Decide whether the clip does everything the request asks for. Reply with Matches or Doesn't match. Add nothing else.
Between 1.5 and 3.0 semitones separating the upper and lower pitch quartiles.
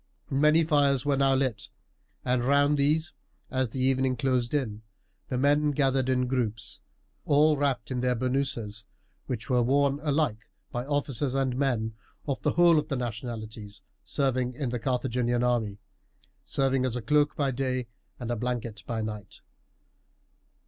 Matches